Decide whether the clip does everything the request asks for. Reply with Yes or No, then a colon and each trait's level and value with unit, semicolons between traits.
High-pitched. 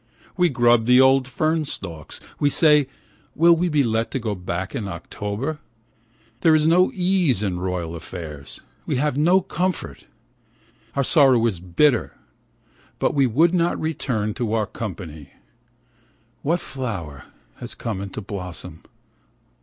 No: low, 125 Hz